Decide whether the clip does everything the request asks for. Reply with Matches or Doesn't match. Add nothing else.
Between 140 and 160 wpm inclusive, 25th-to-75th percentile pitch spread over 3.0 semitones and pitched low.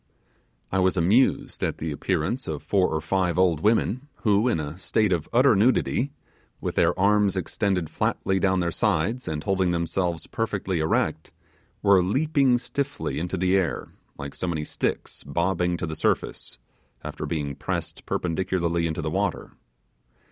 Matches